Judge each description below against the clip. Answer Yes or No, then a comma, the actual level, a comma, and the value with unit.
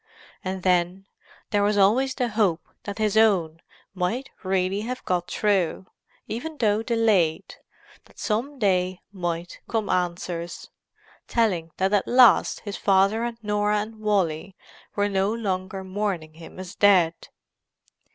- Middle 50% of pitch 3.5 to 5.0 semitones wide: No, average, 3.0 semitones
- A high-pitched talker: Yes, high, 200 Hz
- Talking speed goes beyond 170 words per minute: No, slow, 135 wpm